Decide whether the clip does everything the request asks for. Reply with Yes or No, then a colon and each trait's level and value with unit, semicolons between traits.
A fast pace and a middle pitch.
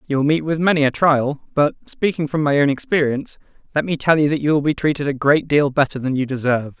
Yes: fast, 255 wpm; medium, 145 Hz